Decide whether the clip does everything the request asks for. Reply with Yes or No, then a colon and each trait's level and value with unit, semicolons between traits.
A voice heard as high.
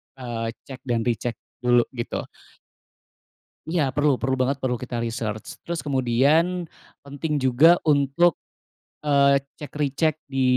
No: low, 135 Hz